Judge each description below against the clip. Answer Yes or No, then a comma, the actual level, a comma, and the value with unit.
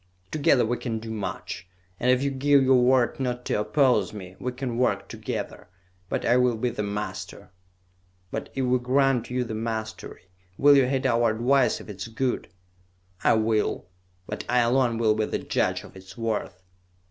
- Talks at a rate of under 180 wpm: No, average, 185 wpm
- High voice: No, low, 120 Hz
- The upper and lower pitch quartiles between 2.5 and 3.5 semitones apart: Yes, average, 2.8 semitones